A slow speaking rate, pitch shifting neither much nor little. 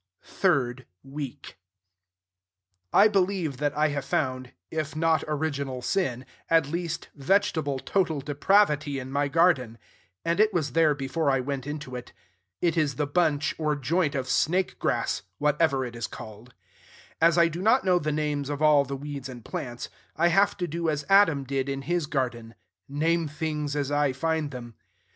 No: average, 165 wpm; average, 3.3 semitones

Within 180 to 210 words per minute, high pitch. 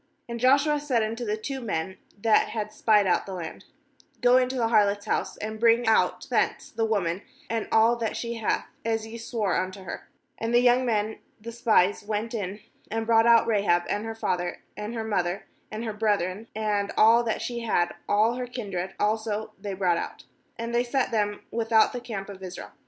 Yes: average, 200 wpm; high, 220 Hz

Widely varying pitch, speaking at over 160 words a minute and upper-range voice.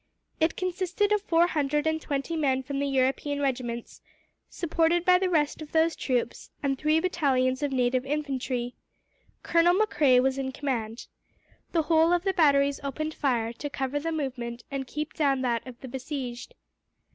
No: average, 3.7 semitones; average, 170 wpm; very high, 280 Hz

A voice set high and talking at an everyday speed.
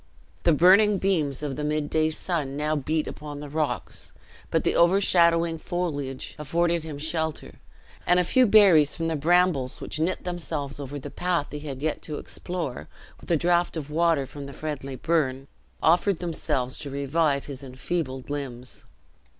No: medium, 155 Hz; average, 165 wpm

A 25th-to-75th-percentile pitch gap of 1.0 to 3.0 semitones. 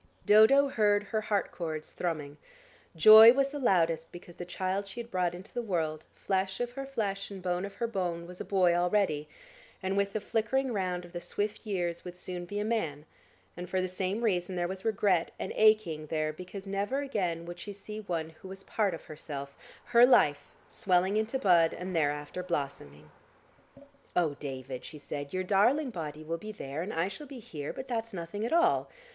No: average, 4.3 semitones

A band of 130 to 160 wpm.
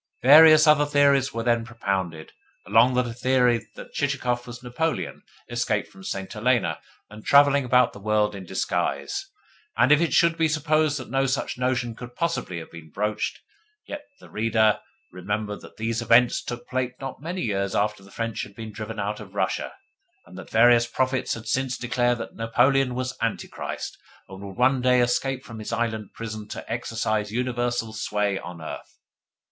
No: average, 175 wpm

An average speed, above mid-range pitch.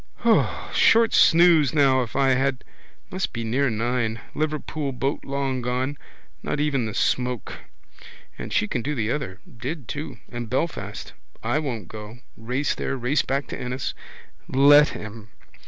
No: average, 150 wpm; low, 130 Hz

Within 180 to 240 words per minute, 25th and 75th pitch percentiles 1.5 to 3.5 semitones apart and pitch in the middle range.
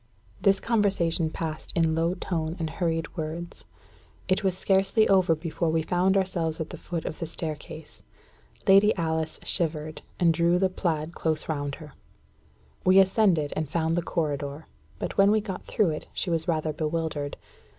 No: average, 170 wpm; average, 2.9 semitones; medium, 165 Hz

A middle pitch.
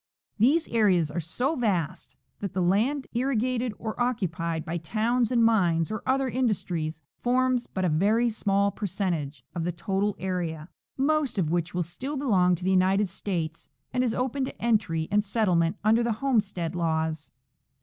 No: high, 200 Hz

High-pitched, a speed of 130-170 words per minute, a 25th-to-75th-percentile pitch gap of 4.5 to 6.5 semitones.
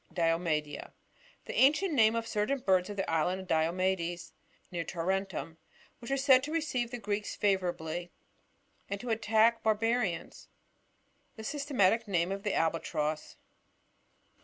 Yes: high, 195 Hz; average, 145 wpm; average, 5.1 semitones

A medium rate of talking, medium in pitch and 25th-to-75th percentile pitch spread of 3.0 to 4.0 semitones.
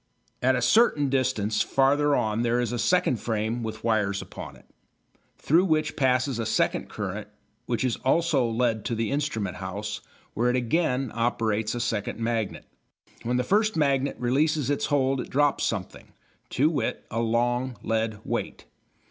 No: average, 165 wpm; low, 120 Hz; average, 3.7 semitones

